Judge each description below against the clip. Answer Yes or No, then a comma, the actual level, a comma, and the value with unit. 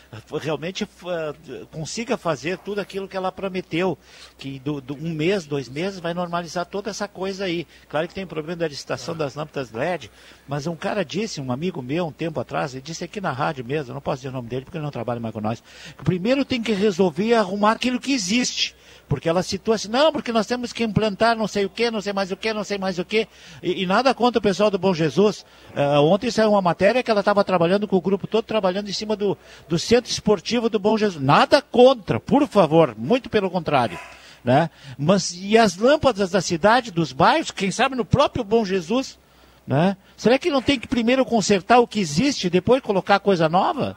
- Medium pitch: No, high, 195 Hz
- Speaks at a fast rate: Yes, fast, 225 wpm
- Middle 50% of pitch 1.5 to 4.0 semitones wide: No, average, 5.1 semitones